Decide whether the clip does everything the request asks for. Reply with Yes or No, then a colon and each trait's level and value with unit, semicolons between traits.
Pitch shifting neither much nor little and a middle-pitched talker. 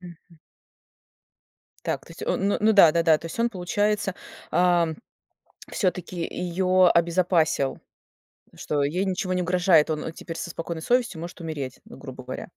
No: narrow, 2.3 semitones; medium, 175 Hz